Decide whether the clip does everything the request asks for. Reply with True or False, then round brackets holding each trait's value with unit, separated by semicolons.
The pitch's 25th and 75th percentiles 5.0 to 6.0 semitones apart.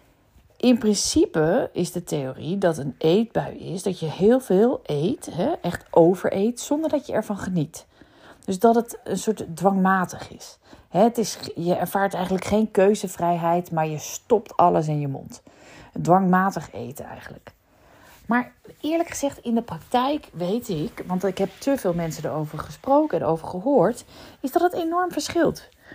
True (5.6 semitones)